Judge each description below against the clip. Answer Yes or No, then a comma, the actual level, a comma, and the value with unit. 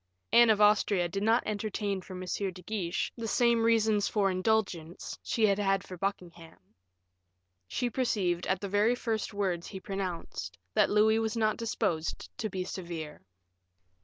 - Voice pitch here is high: Yes, high, 200 Hz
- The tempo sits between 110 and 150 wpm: No, average, 160 wpm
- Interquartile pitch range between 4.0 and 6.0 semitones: No, average, 3.2 semitones